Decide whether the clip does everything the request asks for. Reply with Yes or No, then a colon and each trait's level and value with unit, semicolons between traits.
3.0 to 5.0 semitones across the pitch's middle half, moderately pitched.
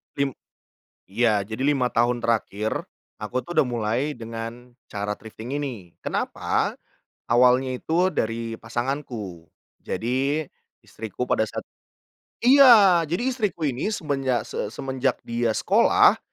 No: average, 4.1 semitones; low, 125 Hz